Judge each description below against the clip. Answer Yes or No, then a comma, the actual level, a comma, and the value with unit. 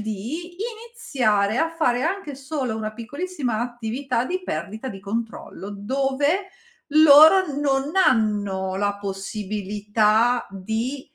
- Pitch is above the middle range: Yes, high, 240 Hz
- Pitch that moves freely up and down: Yes, wide, 6.0 semitones